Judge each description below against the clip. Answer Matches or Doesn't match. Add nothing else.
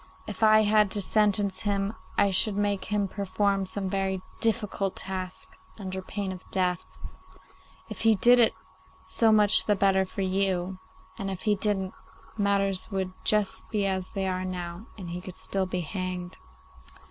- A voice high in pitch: Matches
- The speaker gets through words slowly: Doesn't match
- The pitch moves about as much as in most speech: Doesn't match